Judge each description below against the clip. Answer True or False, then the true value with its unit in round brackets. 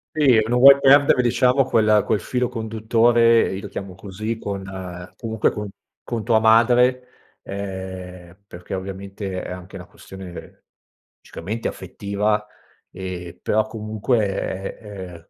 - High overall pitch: False (105 Hz)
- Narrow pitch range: False (3.4 semitones)